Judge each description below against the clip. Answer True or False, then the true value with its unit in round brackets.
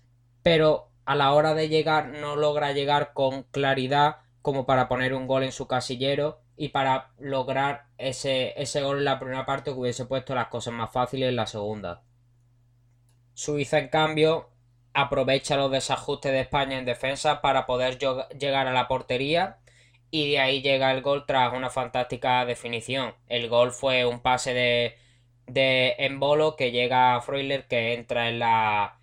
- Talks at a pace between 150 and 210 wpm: True (170 wpm)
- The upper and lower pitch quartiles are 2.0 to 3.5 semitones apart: True (2.4 semitones)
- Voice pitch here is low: True (130 Hz)